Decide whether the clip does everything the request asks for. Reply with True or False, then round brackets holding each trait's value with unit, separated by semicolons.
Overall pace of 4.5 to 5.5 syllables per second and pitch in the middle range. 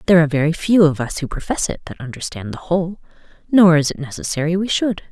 False (6.6 syllables/s; 165 Hz)